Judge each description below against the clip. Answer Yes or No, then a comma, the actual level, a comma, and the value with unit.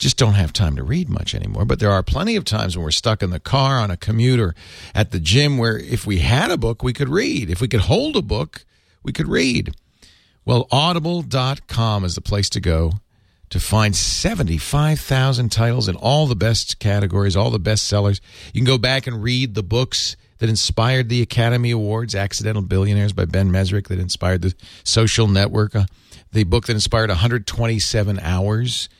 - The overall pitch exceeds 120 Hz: No, low, 110 Hz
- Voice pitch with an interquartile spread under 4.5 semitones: Yes, average, 3.5 semitones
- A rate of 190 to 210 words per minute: Yes, average, 195 wpm